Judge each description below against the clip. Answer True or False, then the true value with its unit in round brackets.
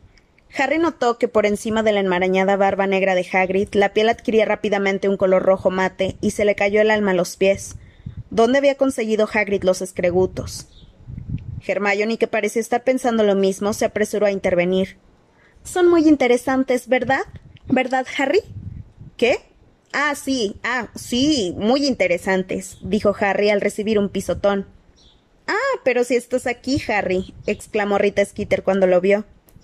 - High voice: True (205 Hz)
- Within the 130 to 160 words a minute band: True (155 wpm)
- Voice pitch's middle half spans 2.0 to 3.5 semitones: False (4.2 semitones)